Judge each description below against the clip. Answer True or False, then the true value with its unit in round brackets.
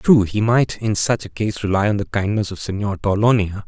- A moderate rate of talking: False (230 wpm)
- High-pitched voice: False (105 Hz)